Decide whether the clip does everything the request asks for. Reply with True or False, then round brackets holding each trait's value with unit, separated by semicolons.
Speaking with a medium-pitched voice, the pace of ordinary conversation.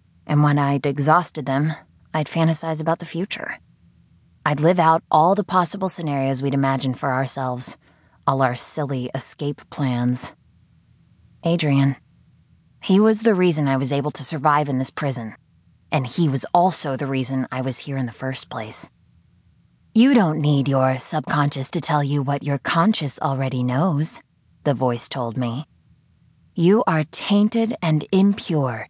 True (145 Hz; 155 wpm)